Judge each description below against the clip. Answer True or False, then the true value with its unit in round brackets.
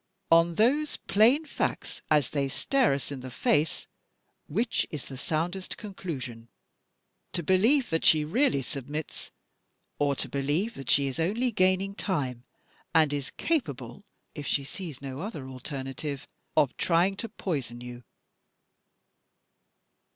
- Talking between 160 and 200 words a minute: False (135 wpm)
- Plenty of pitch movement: True (6.2 semitones)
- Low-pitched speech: False (155 Hz)